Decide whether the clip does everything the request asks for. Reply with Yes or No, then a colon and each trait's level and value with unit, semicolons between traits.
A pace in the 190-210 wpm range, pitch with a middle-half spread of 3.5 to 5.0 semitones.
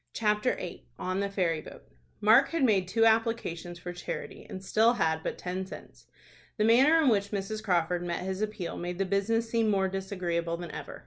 Yes: average, 195 wpm; average, 3.9 semitones